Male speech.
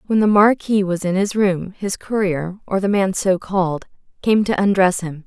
No: female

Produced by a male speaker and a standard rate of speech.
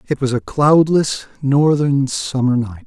Yes: male; average, 145 wpm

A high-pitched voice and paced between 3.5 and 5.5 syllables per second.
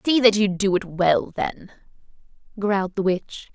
Yes: high, 200 Hz; 4.5 syllables/s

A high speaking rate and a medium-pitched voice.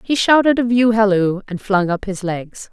No: fast, 220 wpm; high, 210 Hz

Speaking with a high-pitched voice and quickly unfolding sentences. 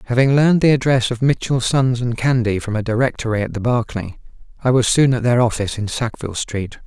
No: low, 120 Hz; fast, 210 wpm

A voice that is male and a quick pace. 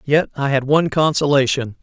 No: male; average, 165 wpm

